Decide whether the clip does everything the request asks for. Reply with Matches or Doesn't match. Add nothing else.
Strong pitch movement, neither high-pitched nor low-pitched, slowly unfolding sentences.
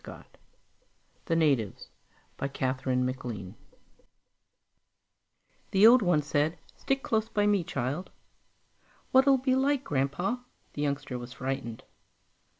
Matches